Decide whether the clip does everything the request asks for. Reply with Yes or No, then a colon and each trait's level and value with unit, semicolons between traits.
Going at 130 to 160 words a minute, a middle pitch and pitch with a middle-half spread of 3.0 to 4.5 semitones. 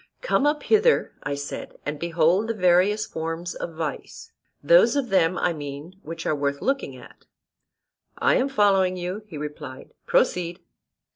No: average, 155 wpm; medium, 175 Hz; average, 5.2 semitones